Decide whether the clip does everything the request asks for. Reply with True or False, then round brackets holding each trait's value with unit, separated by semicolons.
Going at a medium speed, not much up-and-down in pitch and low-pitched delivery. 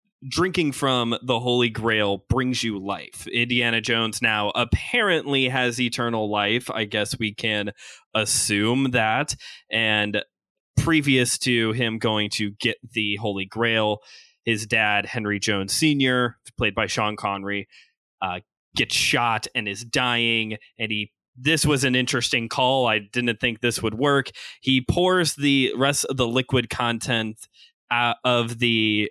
False (145 wpm; 3.0 semitones; 120 Hz)